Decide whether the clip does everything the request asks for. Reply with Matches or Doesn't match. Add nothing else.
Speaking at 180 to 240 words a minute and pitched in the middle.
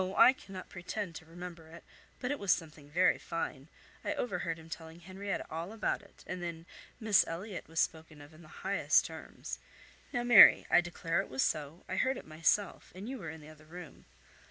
Matches